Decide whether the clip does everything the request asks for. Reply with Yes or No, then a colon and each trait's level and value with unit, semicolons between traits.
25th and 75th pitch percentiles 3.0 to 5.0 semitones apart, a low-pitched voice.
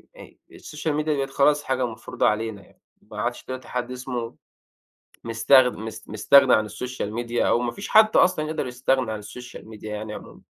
Yes: average, 3.7 semitones; low, 125 Hz